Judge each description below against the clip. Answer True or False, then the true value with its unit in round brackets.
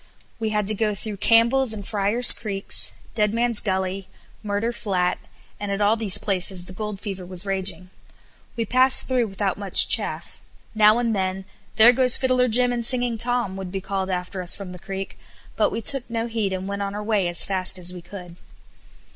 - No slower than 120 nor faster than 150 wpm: False (195 wpm)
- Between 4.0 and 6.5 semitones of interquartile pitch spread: False (3.3 semitones)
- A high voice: True (205 Hz)